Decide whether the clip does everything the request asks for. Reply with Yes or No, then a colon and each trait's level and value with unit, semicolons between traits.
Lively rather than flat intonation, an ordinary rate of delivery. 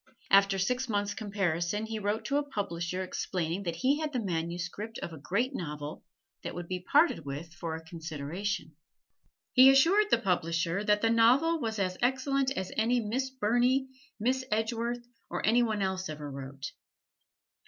Yes: wide, 6.2 semitones; average, 165 wpm